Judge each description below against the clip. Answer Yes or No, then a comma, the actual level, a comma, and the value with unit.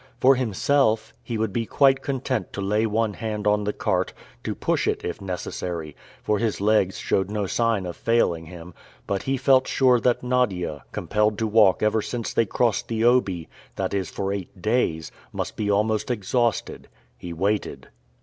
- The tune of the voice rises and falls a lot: No, average, 3.4 semitones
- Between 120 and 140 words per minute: No, average, 180 wpm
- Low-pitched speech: Yes, low, 105 Hz